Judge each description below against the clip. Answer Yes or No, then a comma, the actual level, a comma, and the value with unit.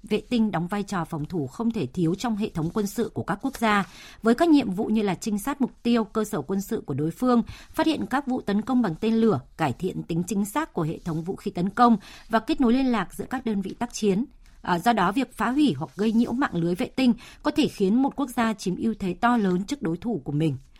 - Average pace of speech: No, fast, 275 wpm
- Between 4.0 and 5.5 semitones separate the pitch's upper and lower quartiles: Yes, average, 4.7 semitones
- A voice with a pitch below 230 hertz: Yes, high, 215 Hz